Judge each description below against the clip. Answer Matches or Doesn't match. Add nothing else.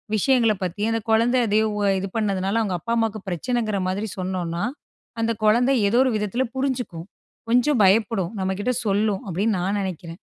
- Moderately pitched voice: Doesn't match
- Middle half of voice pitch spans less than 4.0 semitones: Matches